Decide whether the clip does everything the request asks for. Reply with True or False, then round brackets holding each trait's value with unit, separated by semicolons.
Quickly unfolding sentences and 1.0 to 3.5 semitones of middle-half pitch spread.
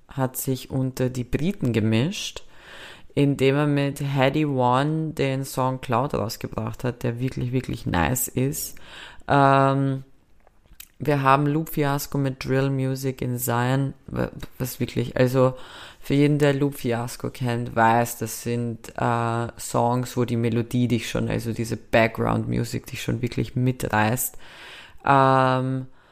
False (135 wpm; 2.4 semitones)